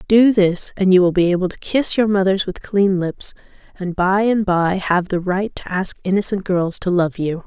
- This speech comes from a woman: Yes, female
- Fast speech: Yes, fast, 225 wpm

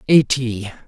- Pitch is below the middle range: Yes, low, 125 Hz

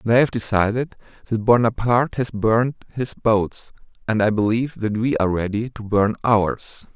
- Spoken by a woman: No, male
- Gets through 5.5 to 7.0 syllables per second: No, 4.8 syllables/s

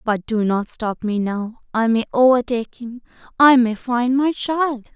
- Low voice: No, high, 240 Hz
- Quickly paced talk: No, average, 155 wpm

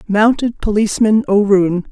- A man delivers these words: No, female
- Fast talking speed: No, slow, 95 wpm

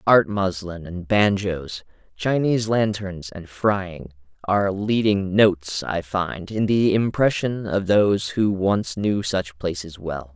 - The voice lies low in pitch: Yes, very low, 95 Hz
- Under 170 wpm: Yes, average, 140 wpm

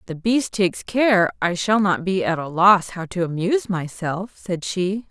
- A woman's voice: Yes, female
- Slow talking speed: No, average, 200 wpm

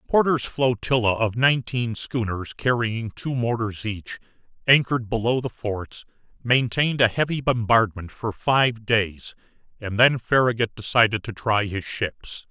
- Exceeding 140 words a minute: No, slow, 135 wpm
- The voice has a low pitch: Yes, low, 115 Hz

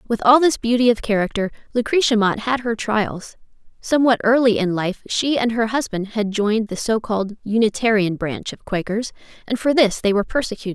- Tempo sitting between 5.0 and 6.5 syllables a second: Yes, 5.5 syllables/s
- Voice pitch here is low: No, high, 220 Hz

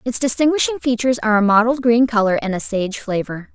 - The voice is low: No, high, 230 Hz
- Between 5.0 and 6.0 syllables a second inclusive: No, 6.2 syllables/s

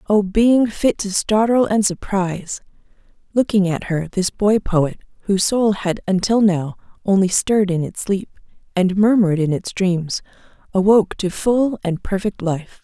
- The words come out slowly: No, average, 160 wpm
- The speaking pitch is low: No, high, 195 Hz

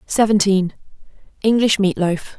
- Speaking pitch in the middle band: No, high, 200 Hz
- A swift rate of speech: No, slow, 75 wpm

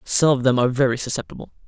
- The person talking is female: No, male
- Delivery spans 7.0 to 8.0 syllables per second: Yes, 7.5 syllables/s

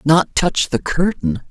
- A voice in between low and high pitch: Yes, medium, 150 Hz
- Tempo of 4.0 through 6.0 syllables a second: No, 3.7 syllables/s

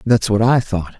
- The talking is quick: Yes, fast, 240 wpm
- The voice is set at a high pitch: No, low, 110 Hz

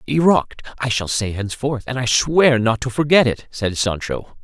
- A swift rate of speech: No, average, 190 wpm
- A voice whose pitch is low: Yes, low, 120 Hz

